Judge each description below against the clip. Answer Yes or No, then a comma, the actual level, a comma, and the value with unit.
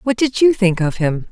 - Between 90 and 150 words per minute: No, fast, 275 wpm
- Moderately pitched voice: No, high, 210 Hz